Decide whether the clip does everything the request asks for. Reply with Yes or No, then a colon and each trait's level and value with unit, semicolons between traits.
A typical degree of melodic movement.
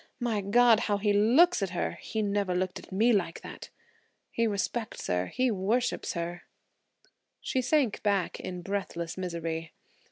Yes: average, 4.3 semitones